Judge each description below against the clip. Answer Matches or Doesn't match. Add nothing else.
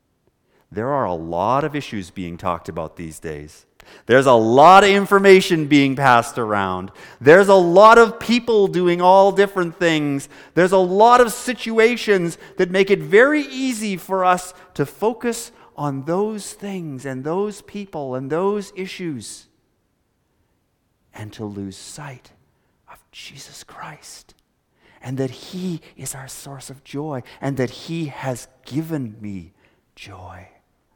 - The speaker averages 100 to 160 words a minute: Matches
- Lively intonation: Matches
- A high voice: Doesn't match